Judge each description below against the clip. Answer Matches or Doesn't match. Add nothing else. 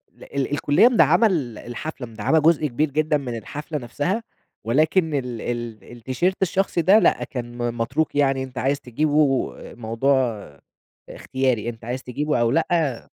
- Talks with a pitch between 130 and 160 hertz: Matches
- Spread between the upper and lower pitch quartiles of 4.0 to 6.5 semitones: Matches